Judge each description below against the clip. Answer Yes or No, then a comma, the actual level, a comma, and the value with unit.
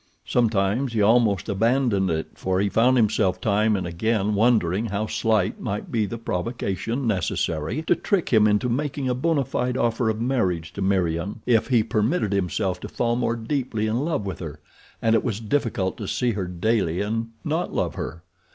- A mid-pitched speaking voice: No, low, 110 Hz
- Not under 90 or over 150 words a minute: No, average, 185 wpm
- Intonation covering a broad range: No, average, 3.7 semitones